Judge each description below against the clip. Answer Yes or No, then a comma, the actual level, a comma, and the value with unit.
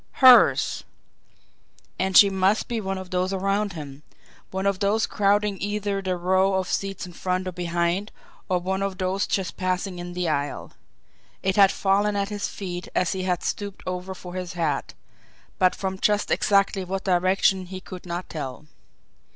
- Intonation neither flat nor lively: No, narrow, 1.6 semitones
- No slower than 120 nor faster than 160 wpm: No, average, 175 wpm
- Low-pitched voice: No, high, 190 Hz